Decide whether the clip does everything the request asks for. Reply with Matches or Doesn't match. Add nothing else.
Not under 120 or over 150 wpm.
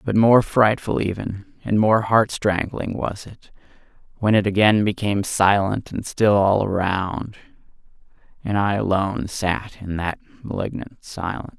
Matches